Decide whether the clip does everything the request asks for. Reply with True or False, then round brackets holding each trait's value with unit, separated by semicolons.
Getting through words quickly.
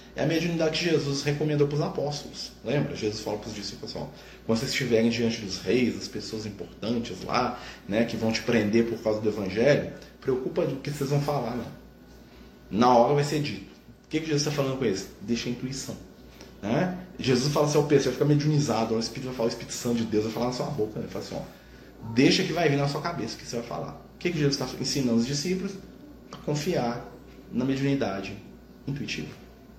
True (225 wpm)